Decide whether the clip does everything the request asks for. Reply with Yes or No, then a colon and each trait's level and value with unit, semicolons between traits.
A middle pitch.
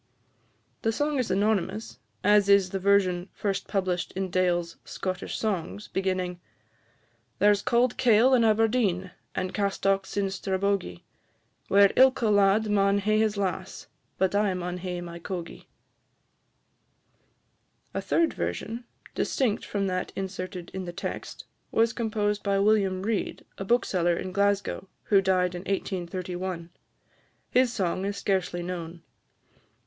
No: high, 195 Hz